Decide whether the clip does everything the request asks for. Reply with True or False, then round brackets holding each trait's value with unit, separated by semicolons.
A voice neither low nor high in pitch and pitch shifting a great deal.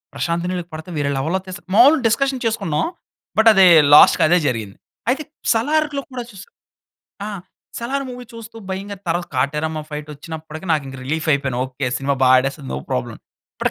True (170 Hz; 8.1 semitones)